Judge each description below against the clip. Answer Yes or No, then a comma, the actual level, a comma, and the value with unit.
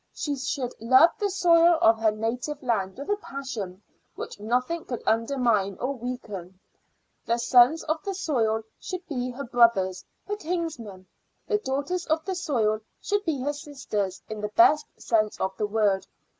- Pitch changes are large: Yes, wide, 6.6 semitones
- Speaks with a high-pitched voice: Yes, very high, 250 Hz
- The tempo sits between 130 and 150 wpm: No, average, 165 wpm